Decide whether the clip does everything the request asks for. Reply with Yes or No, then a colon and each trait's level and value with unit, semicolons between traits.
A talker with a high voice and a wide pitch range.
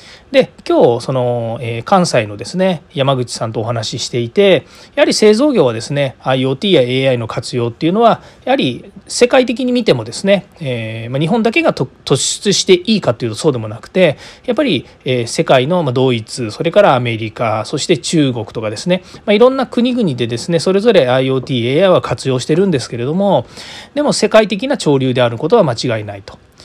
No: medium, 140 Hz; wide, 8.6 semitones